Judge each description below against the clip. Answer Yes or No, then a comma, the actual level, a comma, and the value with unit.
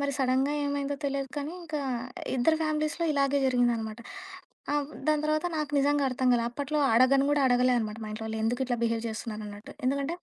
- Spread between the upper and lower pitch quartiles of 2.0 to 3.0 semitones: No, average, 3.6 semitones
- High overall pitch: Yes, very high, 275 Hz